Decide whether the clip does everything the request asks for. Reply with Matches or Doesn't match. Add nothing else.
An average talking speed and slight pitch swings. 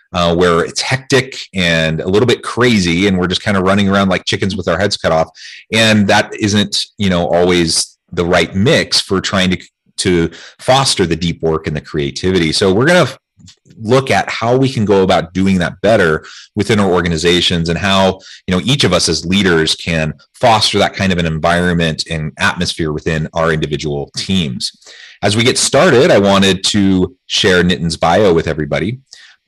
Doesn't match